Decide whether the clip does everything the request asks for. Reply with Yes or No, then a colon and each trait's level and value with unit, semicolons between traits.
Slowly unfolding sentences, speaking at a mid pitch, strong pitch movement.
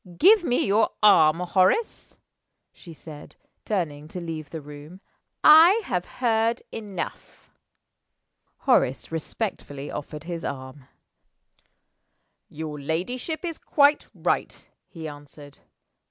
Yes: slow, 105 wpm; medium, 170 Hz; wide, 7.2 semitones